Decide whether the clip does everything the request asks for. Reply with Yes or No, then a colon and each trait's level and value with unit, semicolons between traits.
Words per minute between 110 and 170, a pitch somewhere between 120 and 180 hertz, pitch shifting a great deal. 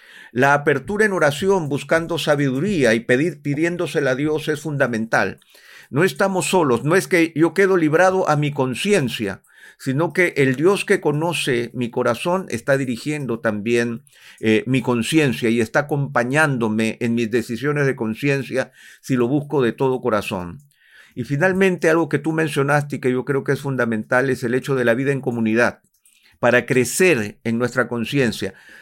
No: average, 165 wpm; medium, 140 Hz; average, 4.8 semitones